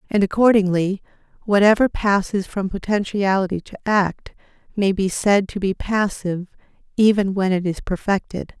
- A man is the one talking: No, female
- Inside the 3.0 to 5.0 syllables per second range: Yes, 4.8 syllables/s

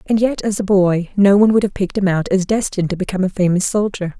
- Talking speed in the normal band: No, fast, 270 wpm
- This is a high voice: Yes, high, 195 Hz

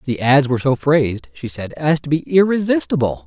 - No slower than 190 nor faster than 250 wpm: Yes, average, 200 wpm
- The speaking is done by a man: Yes, male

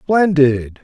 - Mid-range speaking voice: Yes, medium, 150 Hz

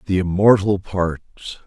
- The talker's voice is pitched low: Yes, very low, 95 Hz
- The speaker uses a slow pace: Yes, slow, 110 wpm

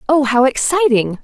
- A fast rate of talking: No, average, 145 wpm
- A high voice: Yes, very high, 265 Hz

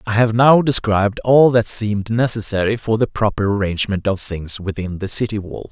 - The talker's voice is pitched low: Yes, low, 105 Hz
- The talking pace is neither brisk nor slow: Yes, average, 190 wpm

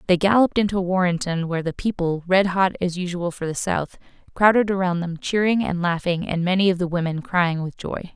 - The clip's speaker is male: No, female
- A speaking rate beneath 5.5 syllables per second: No, 5.6 syllables/s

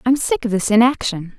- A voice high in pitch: Yes, high, 235 Hz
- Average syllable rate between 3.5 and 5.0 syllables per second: No, 5.6 syllables/s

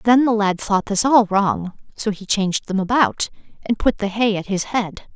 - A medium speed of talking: No, fast, 220 wpm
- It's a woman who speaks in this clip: Yes, female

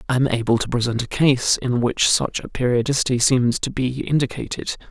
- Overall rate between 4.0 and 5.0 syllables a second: No, 5.5 syllables/s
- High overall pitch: No, low, 125 Hz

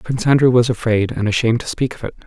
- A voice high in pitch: No, low, 120 Hz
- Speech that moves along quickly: Yes, fast, 265 wpm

